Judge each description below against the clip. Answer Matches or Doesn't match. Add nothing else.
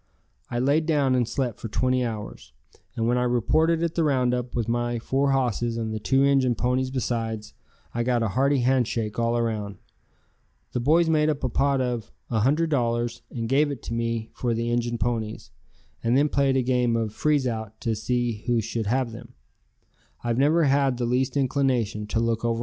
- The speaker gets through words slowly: Doesn't match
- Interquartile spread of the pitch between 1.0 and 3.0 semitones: Matches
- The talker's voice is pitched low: Matches